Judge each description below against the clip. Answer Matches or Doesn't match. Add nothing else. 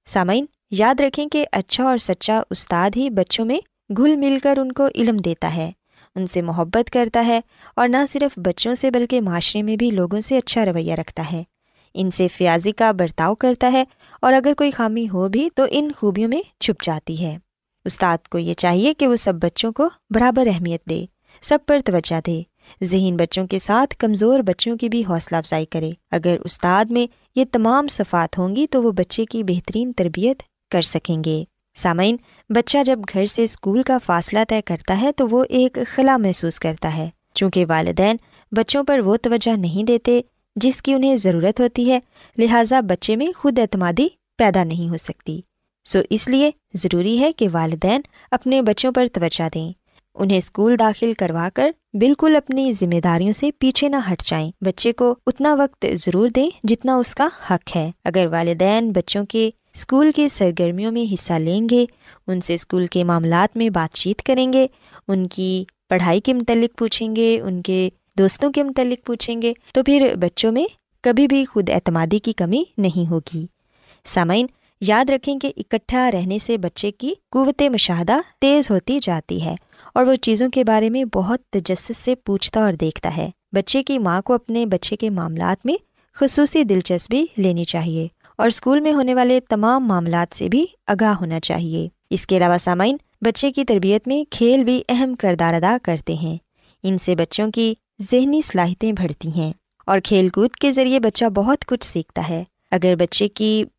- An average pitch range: Doesn't match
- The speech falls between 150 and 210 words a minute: Matches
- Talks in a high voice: Matches